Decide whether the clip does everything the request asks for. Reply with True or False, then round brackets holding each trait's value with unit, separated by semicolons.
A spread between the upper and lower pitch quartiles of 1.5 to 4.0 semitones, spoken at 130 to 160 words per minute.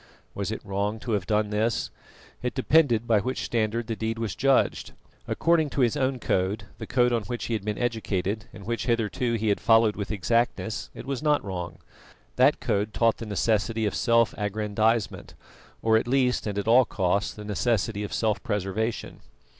False (2.4 semitones; 185 wpm)